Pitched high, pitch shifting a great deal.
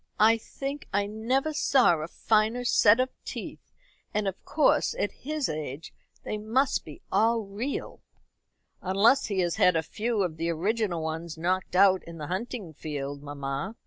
Yes: high, 200 Hz; wide, 5.9 semitones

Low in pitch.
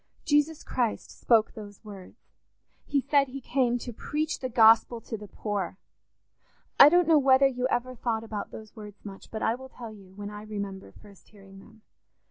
No: high, 225 Hz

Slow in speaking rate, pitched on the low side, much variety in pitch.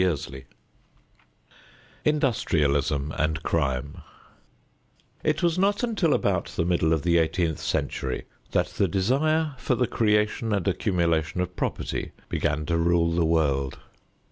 Yes: slow, 125 wpm; very low, 85 Hz; wide, 6.1 semitones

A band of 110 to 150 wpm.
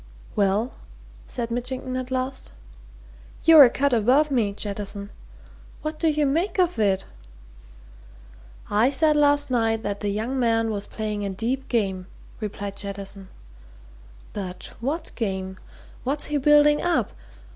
Yes: slow, 135 wpm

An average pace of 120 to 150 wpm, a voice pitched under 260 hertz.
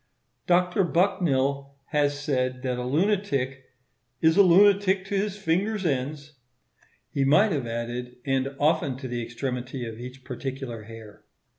Yes: average, 140 wpm; medium, 140 Hz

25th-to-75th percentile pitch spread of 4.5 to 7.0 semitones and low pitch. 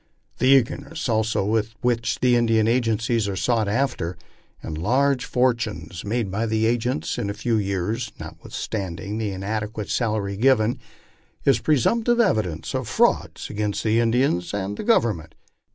No: average, 3.3 semitones; low, 110 Hz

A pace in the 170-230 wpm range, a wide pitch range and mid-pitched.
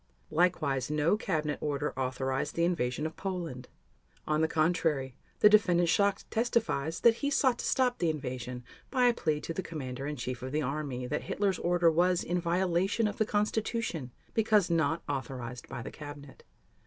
Yes: average, 175 wpm; wide, 5.7 semitones; medium, 160 Hz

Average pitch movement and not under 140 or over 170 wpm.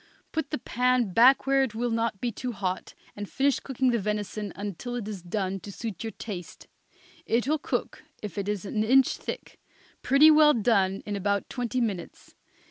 No: average, 3.9 semitones; average, 190 wpm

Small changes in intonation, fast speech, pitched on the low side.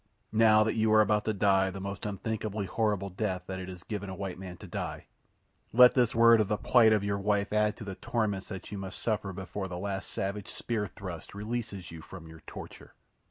Yes: narrow, 2.2 semitones; fast, 215 wpm; low, 100 Hz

